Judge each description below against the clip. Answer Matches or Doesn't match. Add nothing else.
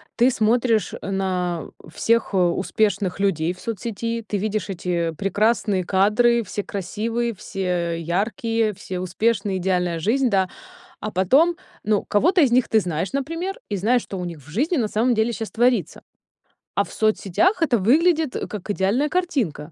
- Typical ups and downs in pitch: Matches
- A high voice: Matches